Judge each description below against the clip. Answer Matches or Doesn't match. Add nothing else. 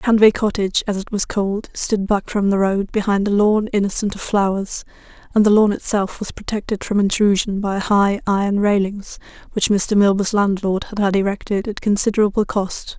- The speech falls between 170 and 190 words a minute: Matches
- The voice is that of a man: Doesn't match